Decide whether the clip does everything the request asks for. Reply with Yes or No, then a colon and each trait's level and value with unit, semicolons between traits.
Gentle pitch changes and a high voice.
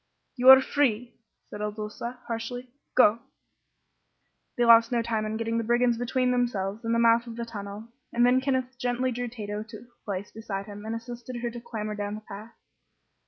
Yes: narrow, 2.3 semitones; high, 230 Hz